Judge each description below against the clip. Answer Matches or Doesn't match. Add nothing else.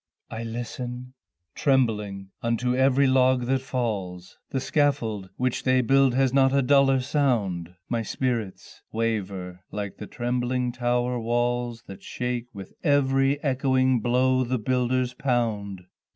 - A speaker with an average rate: Doesn't match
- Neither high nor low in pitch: Doesn't match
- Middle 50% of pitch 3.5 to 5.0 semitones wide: Doesn't match